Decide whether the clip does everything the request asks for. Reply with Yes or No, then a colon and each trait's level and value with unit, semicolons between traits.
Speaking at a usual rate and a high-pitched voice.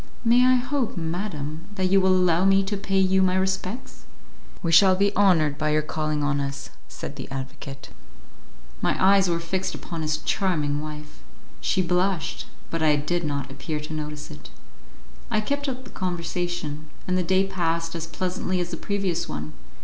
No: average, 180 wpm; medium, 175 Hz